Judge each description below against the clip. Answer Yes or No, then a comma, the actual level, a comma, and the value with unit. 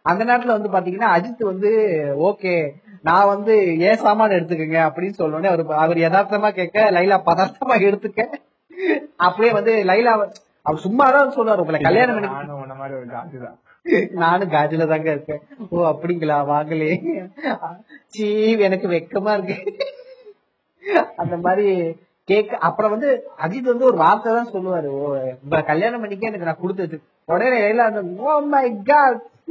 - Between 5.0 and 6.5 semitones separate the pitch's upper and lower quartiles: Yes, wide, 5.4 semitones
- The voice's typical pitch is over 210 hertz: No, high, 195 Hz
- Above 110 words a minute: No, average, 100 wpm